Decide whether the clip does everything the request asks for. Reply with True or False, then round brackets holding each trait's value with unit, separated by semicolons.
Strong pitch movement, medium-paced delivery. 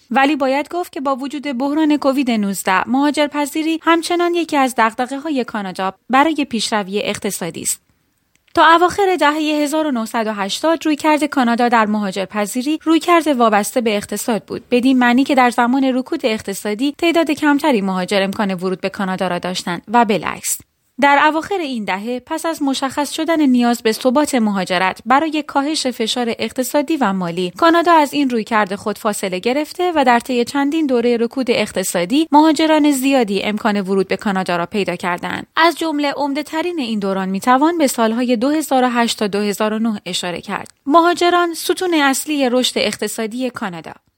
False (6.0 semitones; 160 wpm)